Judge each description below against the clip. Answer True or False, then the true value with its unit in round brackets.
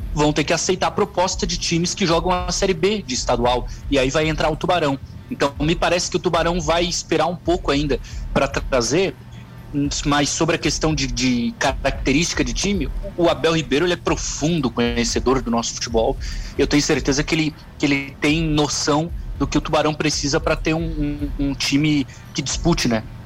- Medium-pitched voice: True (150 Hz)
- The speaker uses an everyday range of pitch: True (3.7 semitones)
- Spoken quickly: True (195 wpm)